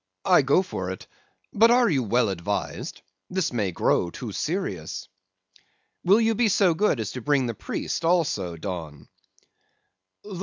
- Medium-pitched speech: No, low, 130 Hz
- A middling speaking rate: Yes, average, 150 wpm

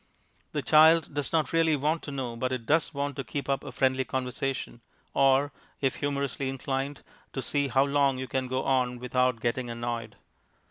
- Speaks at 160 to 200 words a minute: Yes, average, 185 wpm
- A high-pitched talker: No, low, 135 Hz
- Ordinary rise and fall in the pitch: No, narrow, 2.0 semitones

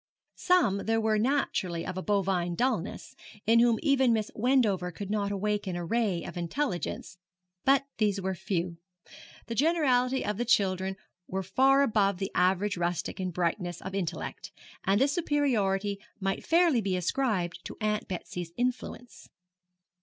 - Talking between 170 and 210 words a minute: No, average, 150 wpm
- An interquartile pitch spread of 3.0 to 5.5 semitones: Yes, average, 4.7 semitones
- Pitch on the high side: Yes, high, 205 Hz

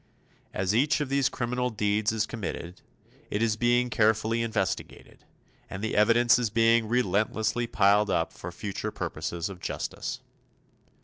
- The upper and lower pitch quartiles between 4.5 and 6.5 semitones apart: No, narrow, 2.6 semitones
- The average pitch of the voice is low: Yes, low, 110 Hz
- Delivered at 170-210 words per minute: No, average, 145 wpm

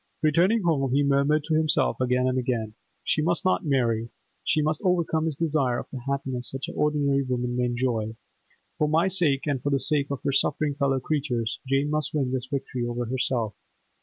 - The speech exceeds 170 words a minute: Yes, average, 195 wpm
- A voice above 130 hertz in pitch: Yes, medium, 140 Hz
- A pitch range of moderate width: Yes, average, 3.3 semitones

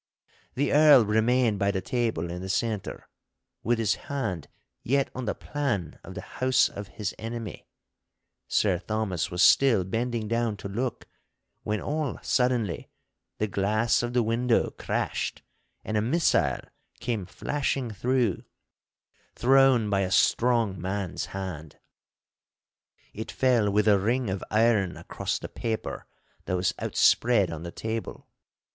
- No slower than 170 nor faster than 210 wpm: No, average, 140 wpm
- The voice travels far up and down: No, average, 4.0 semitones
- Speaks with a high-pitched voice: No, low, 110 Hz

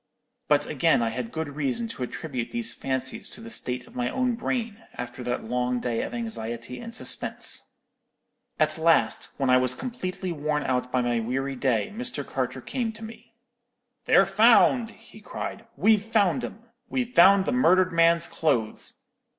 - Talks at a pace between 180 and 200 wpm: No, average, 170 wpm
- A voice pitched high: No, medium, 165 Hz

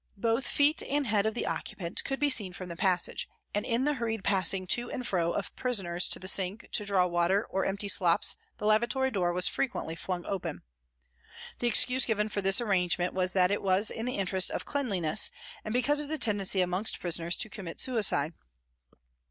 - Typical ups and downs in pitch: Yes, average, 4.4 semitones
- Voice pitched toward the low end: No, high, 200 Hz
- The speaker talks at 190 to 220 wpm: Yes, average, 200 wpm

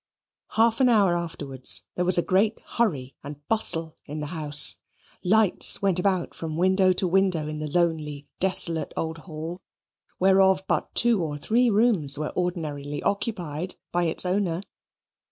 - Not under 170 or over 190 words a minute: No, average, 155 wpm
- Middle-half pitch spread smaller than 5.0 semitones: Yes, average, 4.0 semitones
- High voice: No, medium, 175 Hz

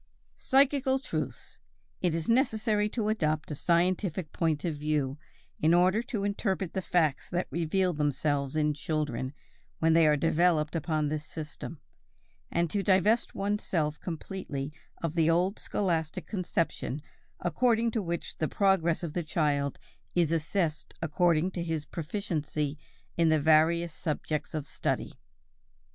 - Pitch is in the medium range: Yes, medium, 165 Hz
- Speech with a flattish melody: No, average, 3.7 semitones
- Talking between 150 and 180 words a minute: No, average, 140 wpm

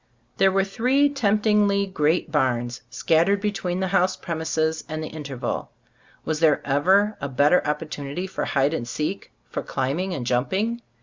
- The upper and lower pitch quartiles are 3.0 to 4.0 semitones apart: No, average, 5.3 semitones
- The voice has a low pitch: No, medium, 165 Hz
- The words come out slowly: No, average, 150 wpm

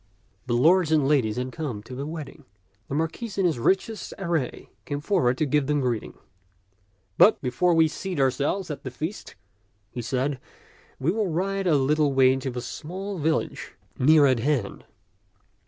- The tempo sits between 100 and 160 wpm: No, average, 170 wpm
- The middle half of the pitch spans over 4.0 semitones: Yes, average, 4.7 semitones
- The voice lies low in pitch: No, medium, 150 Hz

